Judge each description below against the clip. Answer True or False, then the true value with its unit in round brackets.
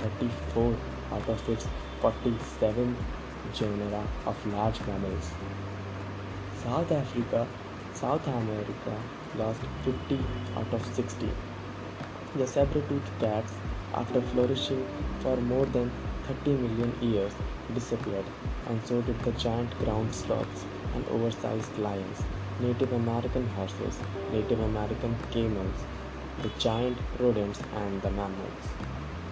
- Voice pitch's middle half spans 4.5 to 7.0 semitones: False (3.5 semitones)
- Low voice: True (110 Hz)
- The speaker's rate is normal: False (105 wpm)